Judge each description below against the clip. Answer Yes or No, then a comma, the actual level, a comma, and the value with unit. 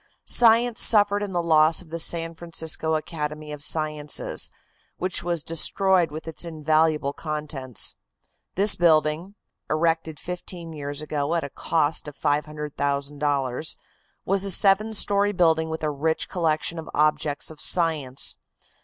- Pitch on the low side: No, medium, 160 Hz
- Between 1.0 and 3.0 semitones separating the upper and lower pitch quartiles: Yes, narrow, 2.4 semitones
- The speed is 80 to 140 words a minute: Yes, slow, 135 wpm